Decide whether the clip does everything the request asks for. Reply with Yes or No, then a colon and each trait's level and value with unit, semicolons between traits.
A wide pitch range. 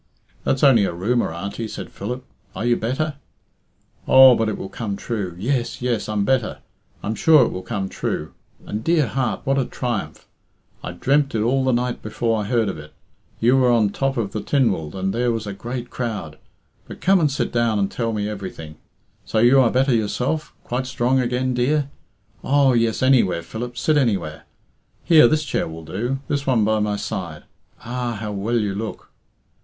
No: average, 4.1 semitones